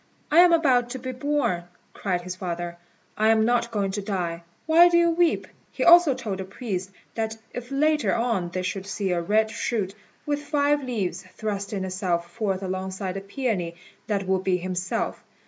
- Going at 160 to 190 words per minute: Yes, average, 185 wpm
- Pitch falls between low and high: No, high, 205 Hz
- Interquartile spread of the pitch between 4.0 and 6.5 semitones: Yes, wide, 5.6 semitones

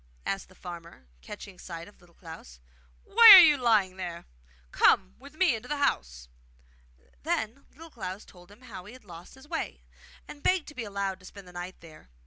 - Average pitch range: No, wide, 6.7 semitones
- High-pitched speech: Yes, high, 195 Hz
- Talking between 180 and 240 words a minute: Yes, average, 195 wpm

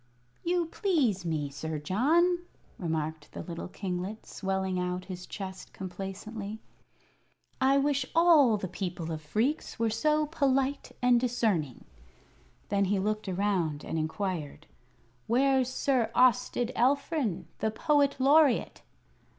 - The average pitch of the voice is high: Yes, high, 215 Hz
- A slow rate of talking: Yes, slow, 120 wpm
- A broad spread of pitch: Yes, wide, 6.9 semitones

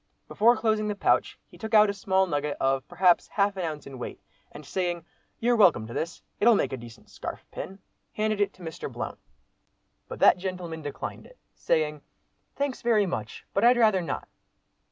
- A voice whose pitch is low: No, medium, 185 Hz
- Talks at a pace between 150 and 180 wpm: No, average, 190 wpm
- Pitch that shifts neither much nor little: No, wide, 5.8 semitones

